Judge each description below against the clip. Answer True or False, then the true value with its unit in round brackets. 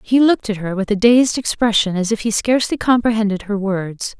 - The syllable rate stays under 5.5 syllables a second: False (5.6 syllables/s)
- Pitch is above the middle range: True (215 Hz)